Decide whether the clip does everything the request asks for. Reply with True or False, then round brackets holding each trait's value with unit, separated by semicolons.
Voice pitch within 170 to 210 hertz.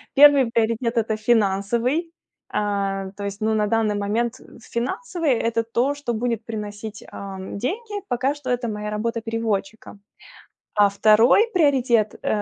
False (225 Hz)